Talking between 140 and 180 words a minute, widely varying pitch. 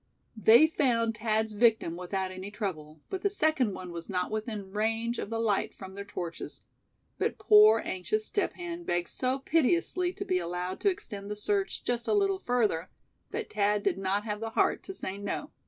No: average, 190 wpm; wide, 7.3 semitones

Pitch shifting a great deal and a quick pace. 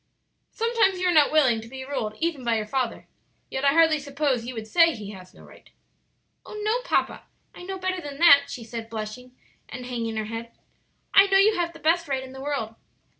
Yes: wide, 6.7 semitones; fast, 220 wpm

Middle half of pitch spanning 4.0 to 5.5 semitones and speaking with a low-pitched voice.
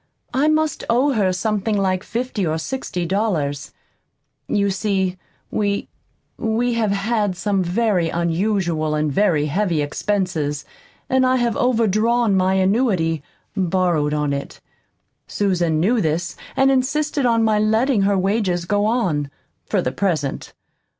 No: average, 4.8 semitones; high, 195 Hz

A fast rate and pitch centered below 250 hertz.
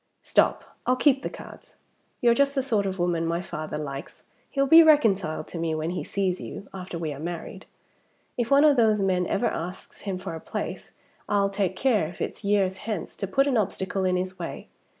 Yes: fast, 210 wpm; high, 190 Hz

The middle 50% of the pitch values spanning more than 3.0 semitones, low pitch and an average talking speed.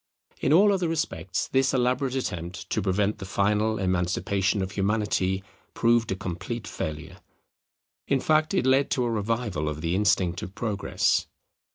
Yes: average, 5.1 semitones; low, 105 Hz; average, 155 wpm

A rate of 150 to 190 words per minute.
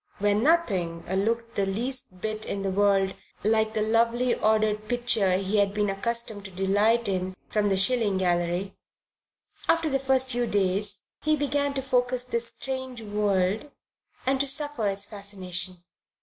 Yes: average, 155 wpm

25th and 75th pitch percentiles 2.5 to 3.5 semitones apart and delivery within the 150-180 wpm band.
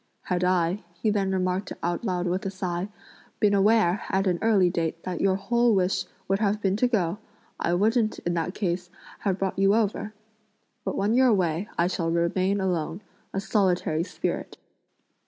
Yes: average, 2.8 semitones; average, 175 wpm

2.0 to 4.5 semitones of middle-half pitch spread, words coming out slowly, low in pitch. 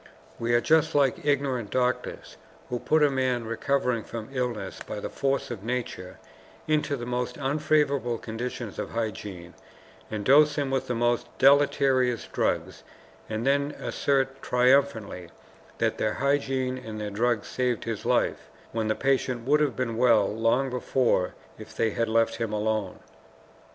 No: average, 3.3 semitones; average, 155 wpm; low, 125 Hz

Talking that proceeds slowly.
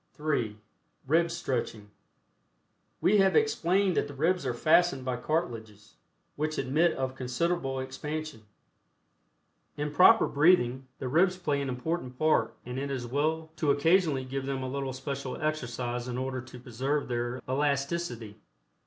No: average, 145 wpm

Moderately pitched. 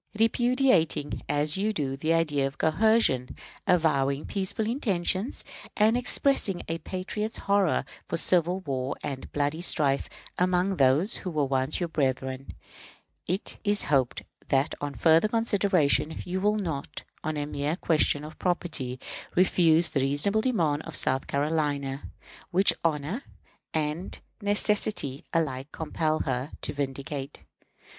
Yes: medium, 160 Hz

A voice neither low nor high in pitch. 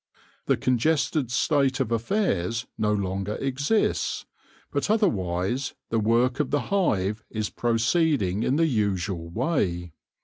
No: low, 115 Hz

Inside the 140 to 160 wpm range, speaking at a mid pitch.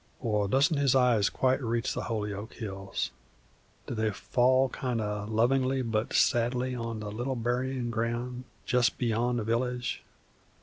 No: average, 145 wpm; low, 120 Hz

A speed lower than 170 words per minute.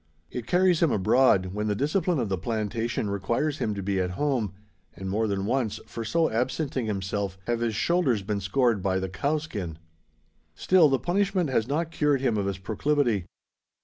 No: average, 180 wpm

